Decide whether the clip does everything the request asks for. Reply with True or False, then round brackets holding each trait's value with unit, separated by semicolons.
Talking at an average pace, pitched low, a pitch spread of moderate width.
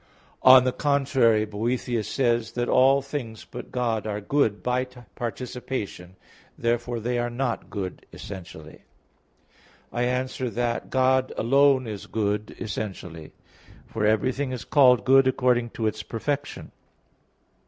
False (130 wpm; 120 Hz; 3.0 semitones)